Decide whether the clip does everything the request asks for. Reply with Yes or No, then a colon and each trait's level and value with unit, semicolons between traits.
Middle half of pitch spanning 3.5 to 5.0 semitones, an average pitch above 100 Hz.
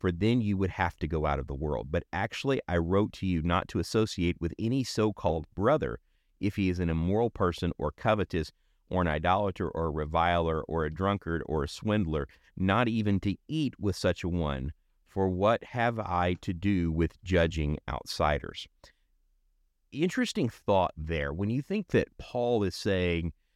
No: average, 4.0 semitones; very low, 90 Hz